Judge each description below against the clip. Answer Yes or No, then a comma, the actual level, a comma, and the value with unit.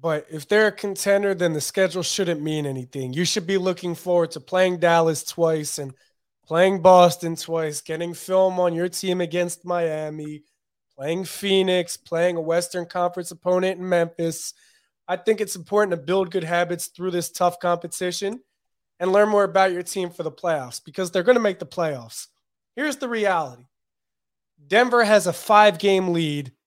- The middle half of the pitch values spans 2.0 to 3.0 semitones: Yes, narrow, 2.5 semitones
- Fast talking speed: No, average, 175 wpm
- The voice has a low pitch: No, medium, 175 Hz